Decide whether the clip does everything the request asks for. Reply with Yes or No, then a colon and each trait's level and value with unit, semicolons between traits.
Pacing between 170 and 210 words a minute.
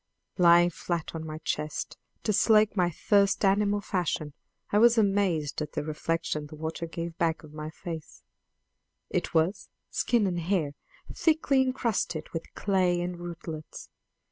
No: average, 145 wpm